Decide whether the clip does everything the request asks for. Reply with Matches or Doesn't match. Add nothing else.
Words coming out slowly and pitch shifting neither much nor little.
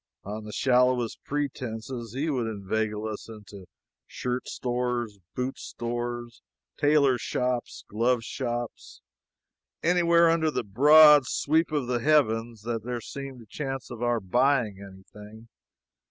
Matches